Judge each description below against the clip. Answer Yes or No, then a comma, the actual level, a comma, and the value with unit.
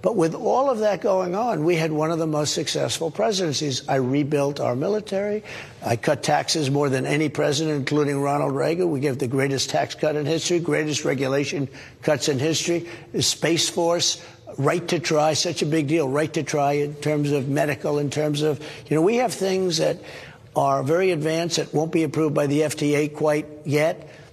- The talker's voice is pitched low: No, medium, 155 Hz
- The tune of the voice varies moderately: No, narrow, 2.3 semitones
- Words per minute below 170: No, average, 195 wpm